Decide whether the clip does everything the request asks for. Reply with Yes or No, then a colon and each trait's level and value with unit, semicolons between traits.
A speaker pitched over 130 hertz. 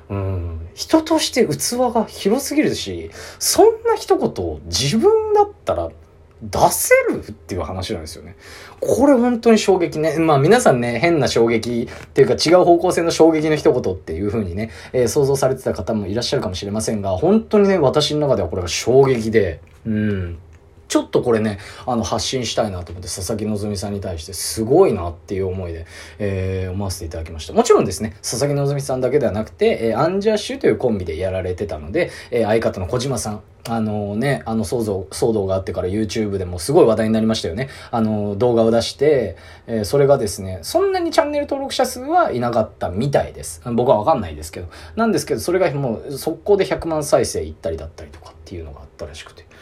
No: low, 115 Hz